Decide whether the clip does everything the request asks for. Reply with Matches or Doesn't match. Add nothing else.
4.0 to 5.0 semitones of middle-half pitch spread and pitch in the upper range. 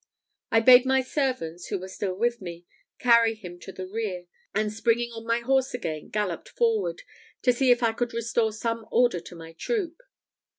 Matches